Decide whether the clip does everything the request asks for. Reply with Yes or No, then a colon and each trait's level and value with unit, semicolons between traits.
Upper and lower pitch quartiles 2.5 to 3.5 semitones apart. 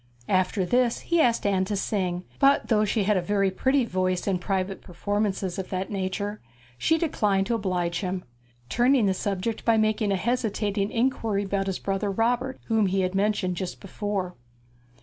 Yes: average, 2.9 semitones